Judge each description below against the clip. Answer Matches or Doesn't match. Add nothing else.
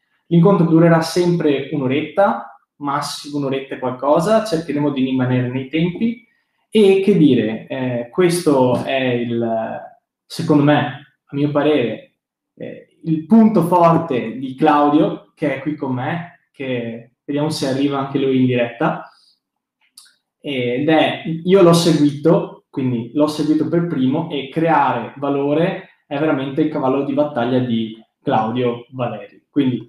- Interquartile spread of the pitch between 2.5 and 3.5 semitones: Doesn't match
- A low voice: Doesn't match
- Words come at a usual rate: Matches